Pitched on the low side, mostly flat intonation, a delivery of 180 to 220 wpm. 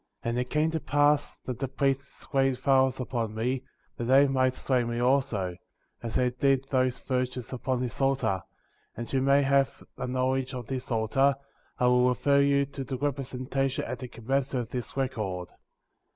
Yes: low, 130 Hz; narrow, 1.7 semitones; average, 185 wpm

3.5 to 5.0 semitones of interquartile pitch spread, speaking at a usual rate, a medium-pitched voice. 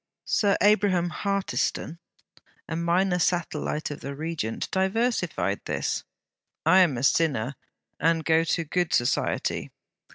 No: average, 3.9 semitones; slow, 120 wpm; medium, 165 Hz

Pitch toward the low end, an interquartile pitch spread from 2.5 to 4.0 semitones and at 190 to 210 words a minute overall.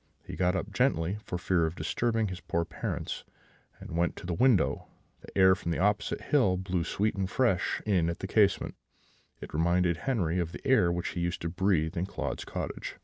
Yes: very low, 90 Hz; average, 2.8 semitones; fast, 205 wpm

